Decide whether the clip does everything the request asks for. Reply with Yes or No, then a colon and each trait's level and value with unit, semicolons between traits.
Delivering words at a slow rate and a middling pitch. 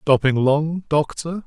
Yes: slow, 125 wpm; medium, 150 Hz